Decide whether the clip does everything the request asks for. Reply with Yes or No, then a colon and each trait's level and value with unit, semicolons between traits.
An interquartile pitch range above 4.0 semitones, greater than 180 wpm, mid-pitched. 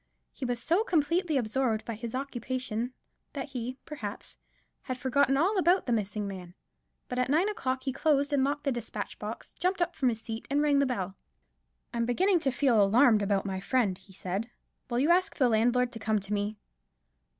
No: average, 4.6 semitones; average, 200 wpm; very high, 250 Hz